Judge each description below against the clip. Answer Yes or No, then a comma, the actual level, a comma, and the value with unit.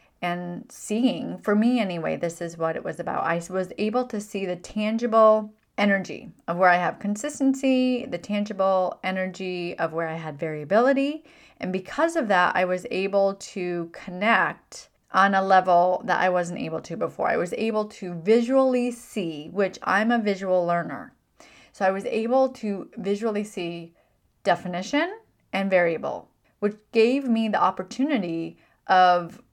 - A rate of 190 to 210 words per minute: No, average, 155 wpm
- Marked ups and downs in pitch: No, average, 4.4 semitones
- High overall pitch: Yes, high, 195 Hz